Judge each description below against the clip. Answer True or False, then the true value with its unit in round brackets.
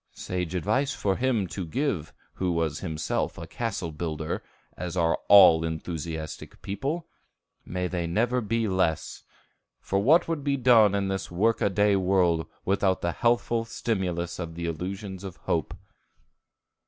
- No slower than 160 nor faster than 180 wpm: False (150 wpm)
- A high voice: False (95 Hz)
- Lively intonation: False (4.9 semitones)